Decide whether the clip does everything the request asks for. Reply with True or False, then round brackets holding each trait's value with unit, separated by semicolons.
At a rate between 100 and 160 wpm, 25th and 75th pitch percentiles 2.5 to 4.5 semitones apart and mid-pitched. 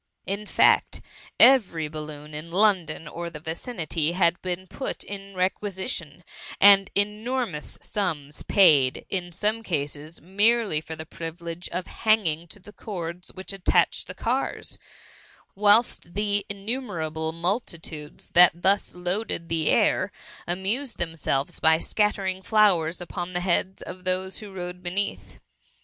True (140 wpm; 3.7 semitones; 180 Hz)